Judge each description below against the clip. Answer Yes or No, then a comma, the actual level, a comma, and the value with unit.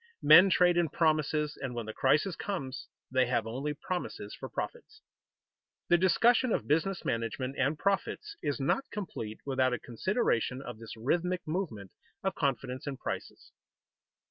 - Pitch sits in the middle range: Yes, medium, 145 Hz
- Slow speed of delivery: No, average, 150 wpm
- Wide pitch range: Yes, wide, 6.0 semitones